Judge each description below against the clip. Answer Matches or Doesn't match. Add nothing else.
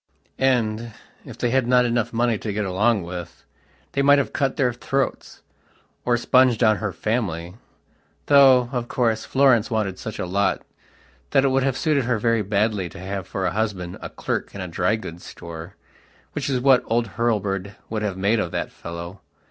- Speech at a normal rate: Matches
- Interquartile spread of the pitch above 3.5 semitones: Matches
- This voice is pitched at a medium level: Doesn't match